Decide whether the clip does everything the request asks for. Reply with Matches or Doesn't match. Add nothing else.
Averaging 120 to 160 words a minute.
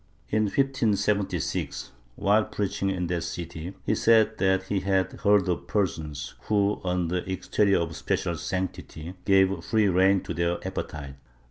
Matches